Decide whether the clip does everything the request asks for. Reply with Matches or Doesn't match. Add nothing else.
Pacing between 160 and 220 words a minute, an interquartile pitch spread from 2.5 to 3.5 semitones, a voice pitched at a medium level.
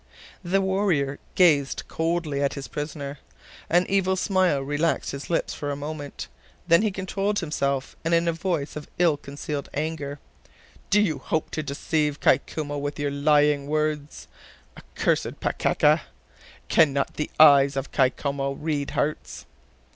Doesn't match